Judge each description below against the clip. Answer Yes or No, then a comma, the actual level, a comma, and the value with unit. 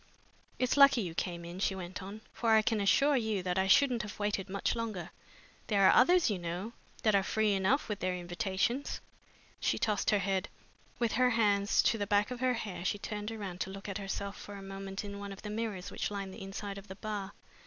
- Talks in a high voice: Yes, high, 200 Hz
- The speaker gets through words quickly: Yes, fast, 230 wpm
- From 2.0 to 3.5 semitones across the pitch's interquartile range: Yes, narrow, 2.4 semitones